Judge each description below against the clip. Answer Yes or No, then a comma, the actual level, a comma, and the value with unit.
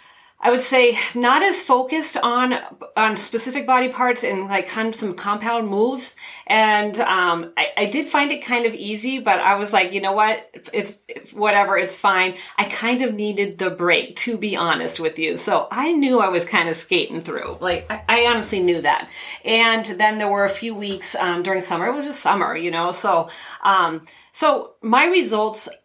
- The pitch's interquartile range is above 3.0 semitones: Yes, average, 4.7 semitones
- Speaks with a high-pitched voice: Yes, high, 215 Hz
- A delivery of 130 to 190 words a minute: No, fast, 205 wpm